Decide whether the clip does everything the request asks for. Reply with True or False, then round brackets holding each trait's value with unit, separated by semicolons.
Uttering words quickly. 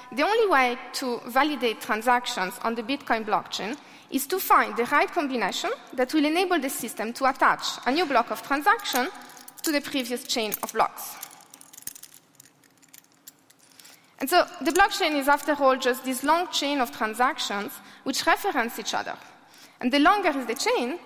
False (160 wpm)